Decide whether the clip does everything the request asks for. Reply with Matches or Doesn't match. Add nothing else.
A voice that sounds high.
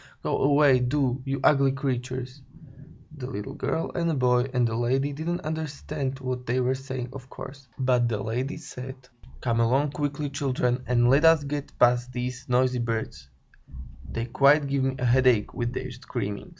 Doesn't match